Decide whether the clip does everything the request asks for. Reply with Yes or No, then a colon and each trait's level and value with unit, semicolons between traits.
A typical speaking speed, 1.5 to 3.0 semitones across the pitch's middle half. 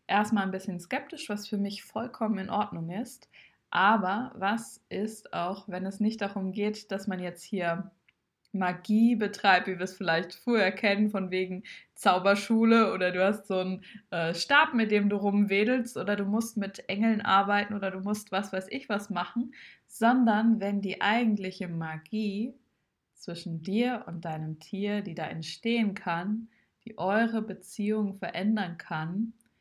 Yes: average, 160 wpm; average, 2.7 semitones